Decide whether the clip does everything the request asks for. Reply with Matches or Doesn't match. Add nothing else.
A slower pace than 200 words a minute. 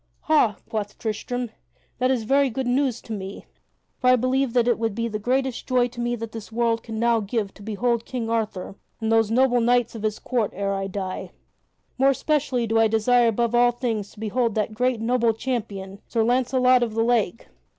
Doesn't match